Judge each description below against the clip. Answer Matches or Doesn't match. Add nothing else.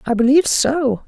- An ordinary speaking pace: Matches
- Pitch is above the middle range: Matches